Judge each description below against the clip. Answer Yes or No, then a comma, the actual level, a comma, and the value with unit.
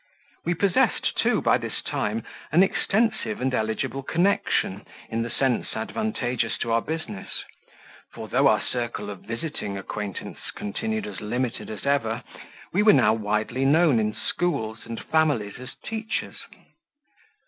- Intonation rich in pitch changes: Yes, wide, 6.9 semitones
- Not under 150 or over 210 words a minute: No, average, 140 wpm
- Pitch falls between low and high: No, low, 125 Hz